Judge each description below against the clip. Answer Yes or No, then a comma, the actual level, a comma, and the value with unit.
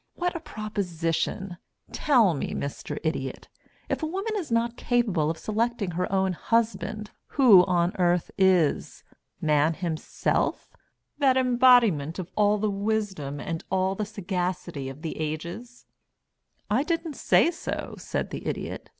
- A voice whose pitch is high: Yes, high, 195 Hz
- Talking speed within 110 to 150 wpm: Yes, average, 140 wpm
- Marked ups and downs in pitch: Yes, wide, 6.0 semitones